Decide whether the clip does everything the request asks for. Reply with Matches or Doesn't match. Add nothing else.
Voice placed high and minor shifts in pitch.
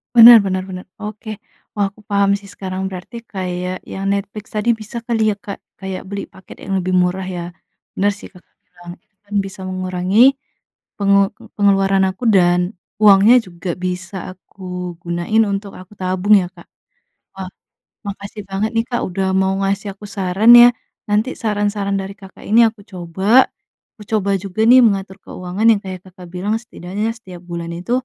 Matches